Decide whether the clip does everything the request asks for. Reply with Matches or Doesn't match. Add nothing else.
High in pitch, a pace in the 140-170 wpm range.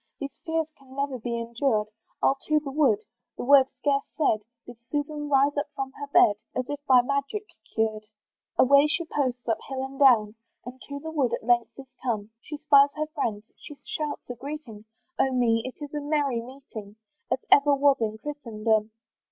Doesn't match